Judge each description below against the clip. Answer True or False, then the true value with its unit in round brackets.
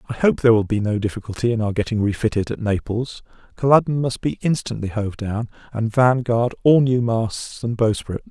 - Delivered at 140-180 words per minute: False (190 wpm)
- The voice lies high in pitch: False (115 Hz)